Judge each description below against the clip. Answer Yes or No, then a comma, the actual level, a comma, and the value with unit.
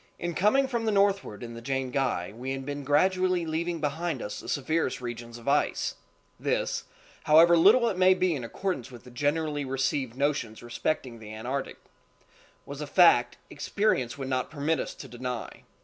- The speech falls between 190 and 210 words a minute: No, average, 165 wpm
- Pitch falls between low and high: Yes, medium, 145 Hz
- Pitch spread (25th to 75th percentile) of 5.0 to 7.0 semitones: Yes, wide, 5.5 semitones